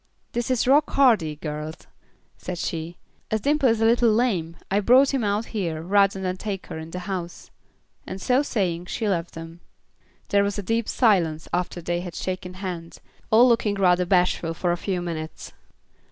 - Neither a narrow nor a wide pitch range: Yes, average, 4.5 semitones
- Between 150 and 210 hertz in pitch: Yes, medium, 185 Hz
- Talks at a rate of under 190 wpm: Yes, average, 180 wpm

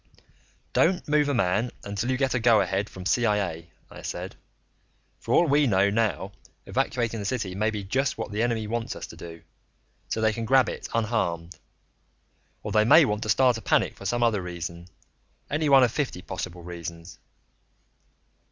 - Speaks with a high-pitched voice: No, low, 110 Hz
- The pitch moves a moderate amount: Yes, average, 4.7 semitones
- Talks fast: No, average, 180 wpm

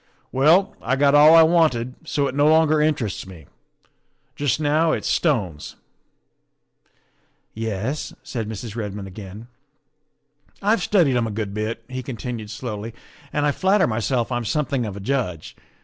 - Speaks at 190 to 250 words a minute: No, average, 160 wpm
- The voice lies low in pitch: Yes, low, 125 Hz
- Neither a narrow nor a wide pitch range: No, wide, 5.7 semitones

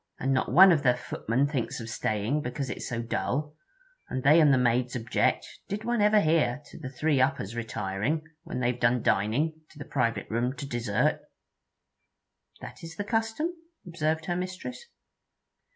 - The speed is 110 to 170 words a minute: No, average, 180 wpm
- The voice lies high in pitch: No, low, 135 Hz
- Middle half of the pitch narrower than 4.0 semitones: No, average, 5.1 semitones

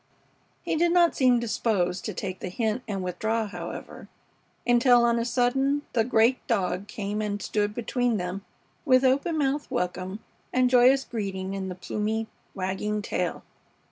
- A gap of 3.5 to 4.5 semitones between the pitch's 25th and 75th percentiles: Yes, average, 4.2 semitones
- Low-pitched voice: No, high, 225 Hz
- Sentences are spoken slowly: No, average, 155 wpm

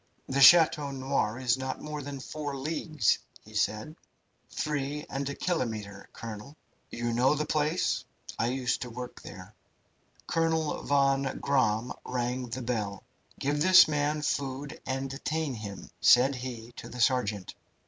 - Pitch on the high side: No, low, 135 Hz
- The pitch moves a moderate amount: Yes, average, 3.8 semitones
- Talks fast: No, average, 145 wpm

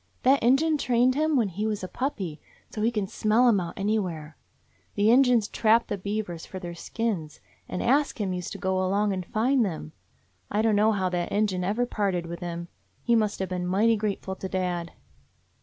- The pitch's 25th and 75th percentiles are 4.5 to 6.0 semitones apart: No, average, 4.0 semitones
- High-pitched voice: Yes, high, 205 Hz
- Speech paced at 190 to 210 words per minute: Yes, average, 195 wpm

